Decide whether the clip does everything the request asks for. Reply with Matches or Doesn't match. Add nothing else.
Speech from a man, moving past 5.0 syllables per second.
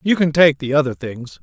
Matches